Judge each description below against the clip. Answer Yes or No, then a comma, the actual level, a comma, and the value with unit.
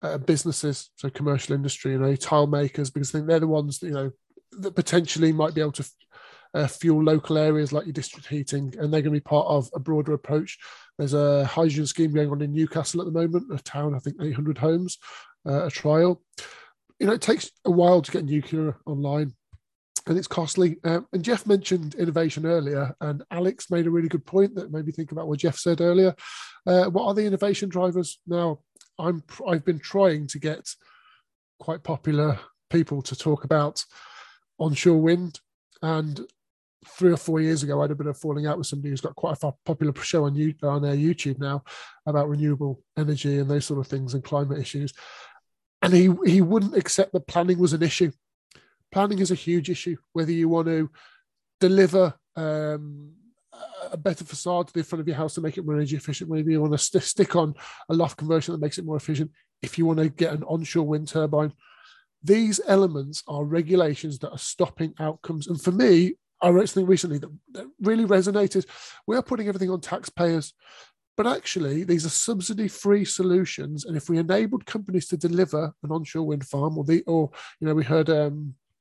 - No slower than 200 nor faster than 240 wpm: Yes, fast, 205 wpm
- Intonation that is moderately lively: Yes, average, 3.3 semitones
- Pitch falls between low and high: Yes, medium, 160 Hz